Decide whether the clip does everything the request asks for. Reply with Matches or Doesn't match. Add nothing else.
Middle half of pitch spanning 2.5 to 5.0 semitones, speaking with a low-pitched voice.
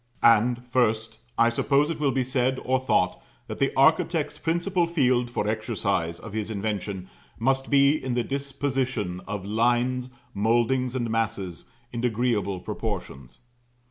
Matches